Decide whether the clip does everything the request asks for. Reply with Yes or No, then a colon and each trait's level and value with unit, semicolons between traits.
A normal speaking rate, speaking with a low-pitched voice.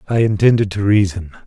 Yes: average, 165 wpm; low, 100 Hz